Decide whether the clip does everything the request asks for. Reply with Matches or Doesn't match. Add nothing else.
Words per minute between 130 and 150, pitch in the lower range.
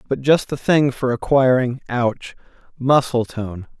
Matches